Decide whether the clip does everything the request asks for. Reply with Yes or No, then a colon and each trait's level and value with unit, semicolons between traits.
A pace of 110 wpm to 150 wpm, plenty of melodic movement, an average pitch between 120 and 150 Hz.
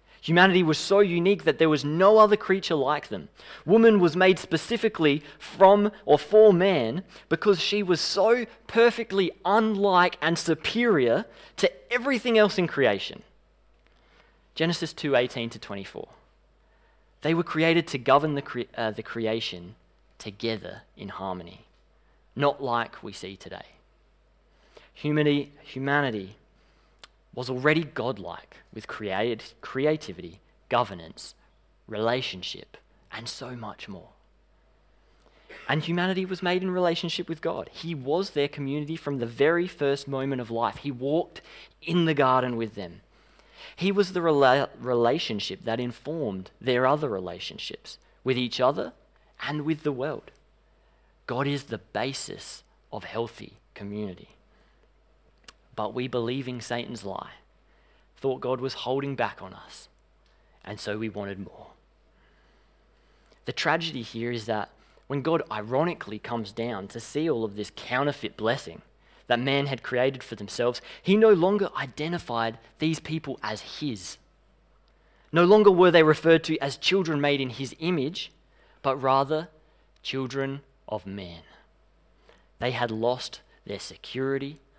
Yes: slow, 135 wpm; wide, 6.4 semitones; medium, 140 Hz